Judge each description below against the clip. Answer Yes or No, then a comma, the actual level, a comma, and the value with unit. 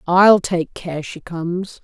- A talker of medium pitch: Yes, medium, 180 Hz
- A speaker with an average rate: Yes, average, 165 wpm